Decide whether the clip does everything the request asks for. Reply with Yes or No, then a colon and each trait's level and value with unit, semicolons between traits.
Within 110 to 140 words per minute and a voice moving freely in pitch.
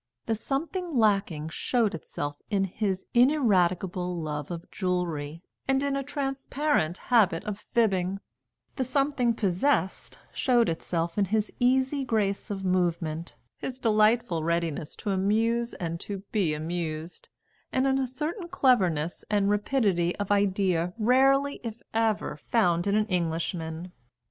Yes: slow, 135 wpm; wide, 6.1 semitones